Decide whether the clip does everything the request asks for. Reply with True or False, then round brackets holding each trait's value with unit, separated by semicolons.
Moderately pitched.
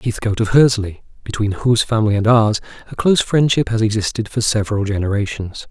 False (110 Hz)